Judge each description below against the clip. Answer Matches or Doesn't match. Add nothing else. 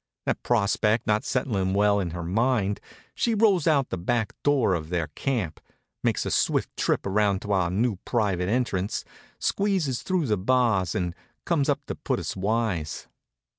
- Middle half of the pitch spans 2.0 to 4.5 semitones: Doesn't match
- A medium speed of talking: Matches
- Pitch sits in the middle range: Doesn't match